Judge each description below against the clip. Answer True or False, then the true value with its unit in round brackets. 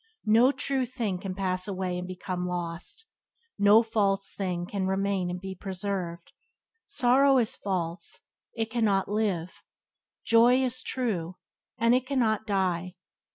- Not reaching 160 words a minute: True (140 wpm)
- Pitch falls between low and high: False (195 Hz)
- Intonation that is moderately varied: True (3.9 semitones)